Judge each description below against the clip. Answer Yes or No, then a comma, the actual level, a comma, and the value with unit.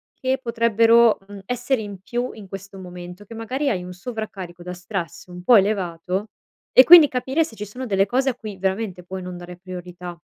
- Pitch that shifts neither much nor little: Yes, average, 4.6 semitones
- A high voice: Yes, high, 200 Hz